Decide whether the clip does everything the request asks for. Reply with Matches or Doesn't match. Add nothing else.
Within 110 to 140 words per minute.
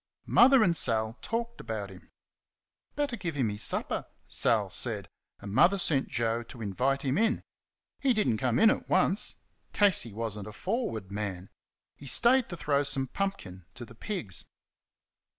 Doesn't match